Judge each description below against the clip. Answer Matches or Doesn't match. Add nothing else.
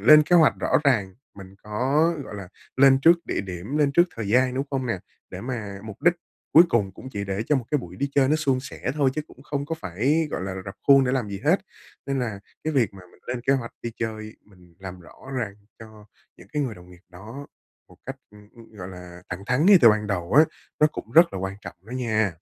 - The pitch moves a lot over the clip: Matches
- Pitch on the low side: Matches